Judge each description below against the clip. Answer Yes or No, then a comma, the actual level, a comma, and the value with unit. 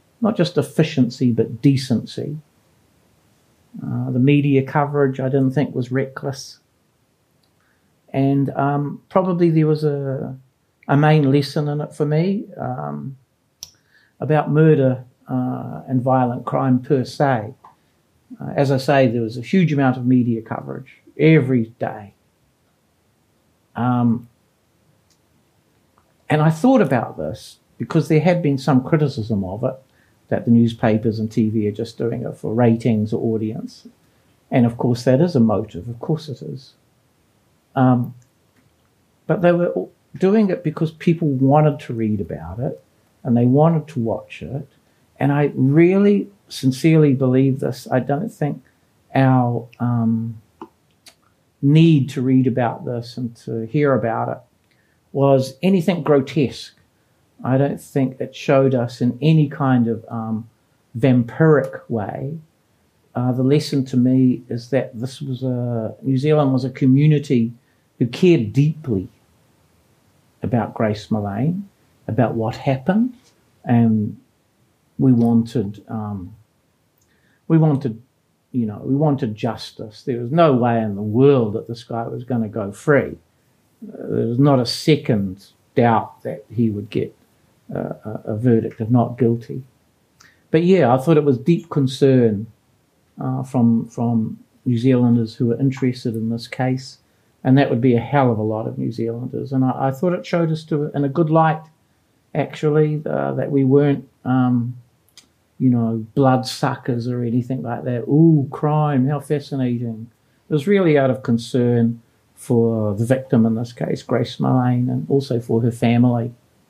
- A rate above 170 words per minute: No, average, 150 wpm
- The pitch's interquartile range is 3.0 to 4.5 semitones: Yes, average, 3.7 semitones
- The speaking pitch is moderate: No, low, 130 Hz